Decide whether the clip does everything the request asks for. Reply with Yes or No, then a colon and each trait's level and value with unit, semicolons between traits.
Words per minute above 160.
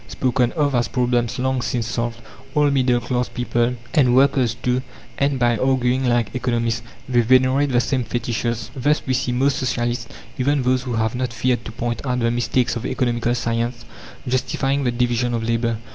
Yes: average, 180 wpm